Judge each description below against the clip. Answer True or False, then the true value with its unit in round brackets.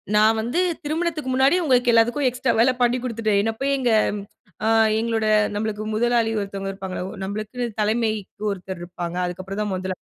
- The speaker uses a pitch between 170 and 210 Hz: False (220 Hz)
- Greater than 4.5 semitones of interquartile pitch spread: False (3.6 semitones)